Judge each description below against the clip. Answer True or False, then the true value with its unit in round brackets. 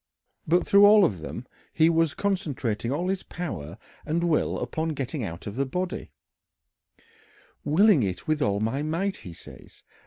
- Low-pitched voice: False (155 Hz)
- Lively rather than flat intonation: True (7.3 semitones)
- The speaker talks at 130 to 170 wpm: True (160 wpm)